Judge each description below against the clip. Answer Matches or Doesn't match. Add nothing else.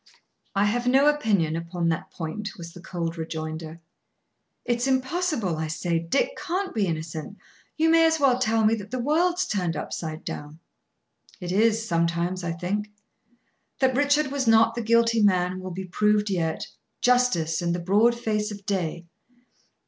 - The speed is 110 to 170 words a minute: Matches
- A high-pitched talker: Matches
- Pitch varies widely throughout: Matches